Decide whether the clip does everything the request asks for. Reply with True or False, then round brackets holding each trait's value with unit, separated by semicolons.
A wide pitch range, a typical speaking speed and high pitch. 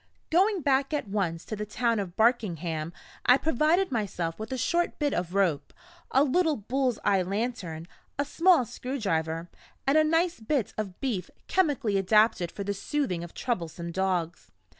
True (7.5 semitones; 160 wpm; 220 Hz)